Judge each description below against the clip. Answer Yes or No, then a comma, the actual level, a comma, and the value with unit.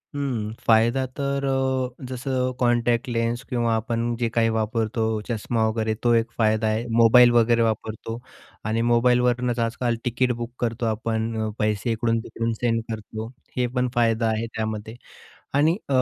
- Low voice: Yes, low, 115 Hz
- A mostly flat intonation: Yes, narrow, 1.7 semitones